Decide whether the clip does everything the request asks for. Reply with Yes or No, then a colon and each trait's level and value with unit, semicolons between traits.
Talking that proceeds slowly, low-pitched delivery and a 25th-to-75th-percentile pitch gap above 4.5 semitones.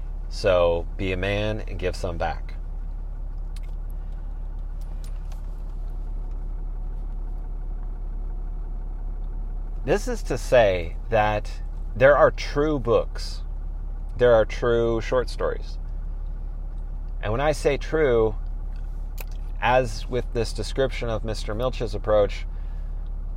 Yes: slow, 90 wpm; very low, 80 Hz; wide, 5.6 semitones